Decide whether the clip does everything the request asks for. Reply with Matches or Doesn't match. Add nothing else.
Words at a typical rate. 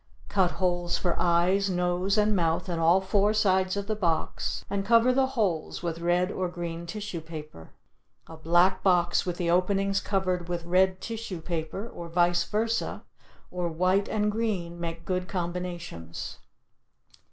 Matches